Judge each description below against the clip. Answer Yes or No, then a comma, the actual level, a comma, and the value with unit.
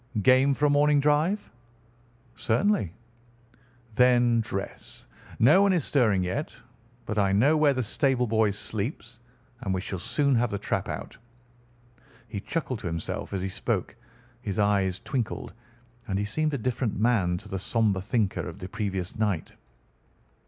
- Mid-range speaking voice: No, low, 115 Hz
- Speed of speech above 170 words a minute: No, average, 155 wpm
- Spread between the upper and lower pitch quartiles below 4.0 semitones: No, wide, 5.4 semitones